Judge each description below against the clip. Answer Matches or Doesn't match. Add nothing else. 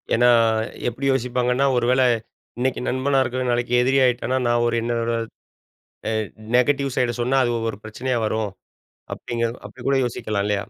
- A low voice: Matches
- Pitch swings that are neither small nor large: Doesn't match